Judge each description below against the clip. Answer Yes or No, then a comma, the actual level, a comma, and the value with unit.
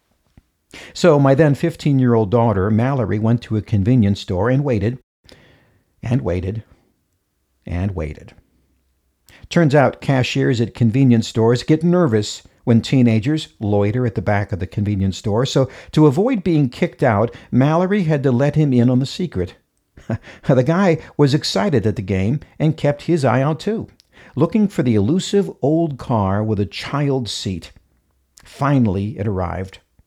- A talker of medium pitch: No, low, 120 Hz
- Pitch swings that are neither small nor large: No, wide, 6.2 semitones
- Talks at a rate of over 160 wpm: No, average, 155 wpm